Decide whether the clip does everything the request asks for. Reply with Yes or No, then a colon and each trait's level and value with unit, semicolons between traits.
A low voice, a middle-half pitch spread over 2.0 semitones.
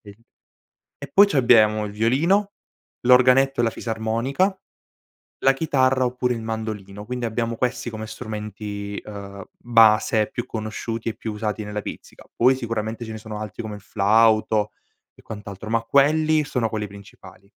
Yes: low, 110 Hz; average, 2.9 semitones